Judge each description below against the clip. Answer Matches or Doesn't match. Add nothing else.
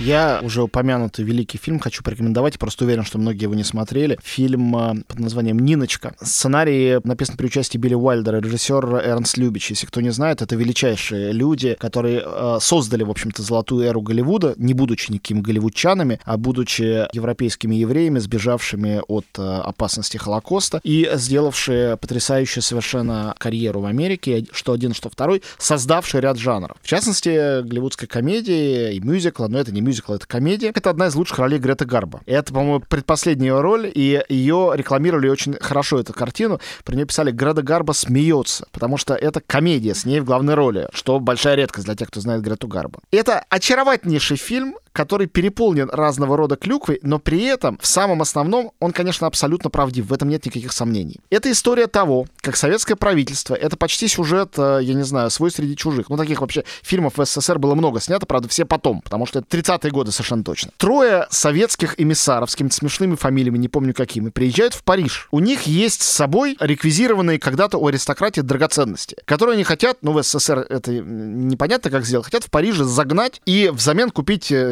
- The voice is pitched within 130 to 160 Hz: Matches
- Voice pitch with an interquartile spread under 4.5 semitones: Doesn't match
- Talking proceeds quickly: Matches